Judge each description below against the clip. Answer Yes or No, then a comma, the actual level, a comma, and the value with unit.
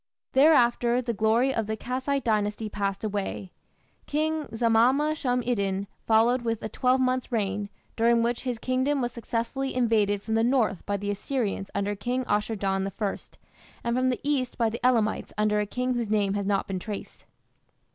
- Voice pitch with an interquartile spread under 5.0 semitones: Yes, average, 3.5 semitones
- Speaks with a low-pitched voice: No, high, 230 Hz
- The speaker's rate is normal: Yes, average, 175 wpm